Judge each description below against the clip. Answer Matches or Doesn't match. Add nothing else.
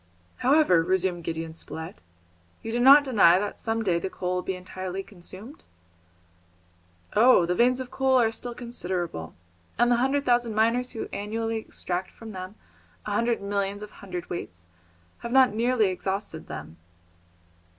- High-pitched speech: Matches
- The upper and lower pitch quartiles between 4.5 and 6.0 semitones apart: Matches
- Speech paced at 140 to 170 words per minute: Matches